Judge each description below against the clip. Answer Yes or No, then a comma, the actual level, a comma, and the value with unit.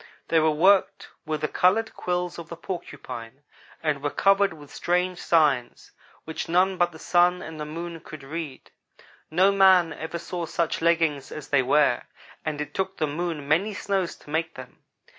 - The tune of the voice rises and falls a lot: No, average, 3.0 semitones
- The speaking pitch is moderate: Yes, medium, 165 Hz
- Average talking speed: Yes, average, 180 wpm